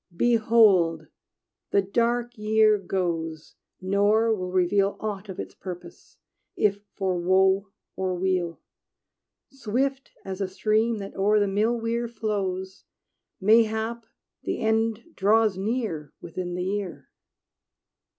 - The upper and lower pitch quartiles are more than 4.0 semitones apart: No, average, 3.0 semitones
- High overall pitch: Yes, high, 200 Hz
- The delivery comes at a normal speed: No, slow, 115 wpm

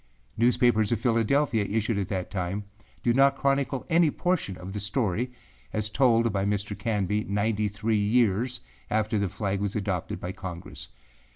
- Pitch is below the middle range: Yes, low, 105 Hz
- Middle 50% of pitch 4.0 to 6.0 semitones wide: No, average, 3.2 semitones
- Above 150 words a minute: Yes, average, 160 wpm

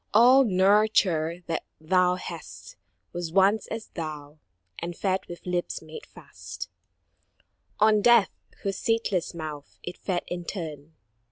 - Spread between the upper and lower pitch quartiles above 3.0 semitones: Yes, average, 4.1 semitones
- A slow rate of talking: Yes, slow, 125 wpm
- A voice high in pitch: No, medium, 180 Hz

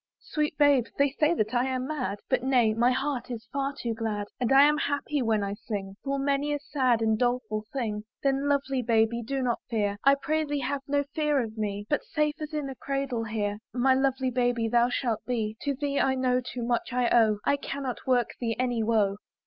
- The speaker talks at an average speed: No, fast, 220 wpm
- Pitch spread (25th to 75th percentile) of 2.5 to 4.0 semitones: Yes, average, 3.7 semitones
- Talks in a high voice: Yes, very high, 250 Hz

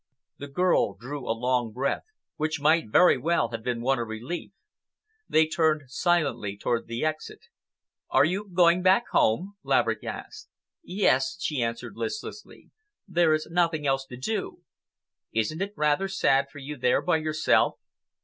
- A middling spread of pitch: No, wide, 5.7 semitones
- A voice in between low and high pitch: Yes, medium, 150 Hz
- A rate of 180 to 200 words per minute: No, average, 155 wpm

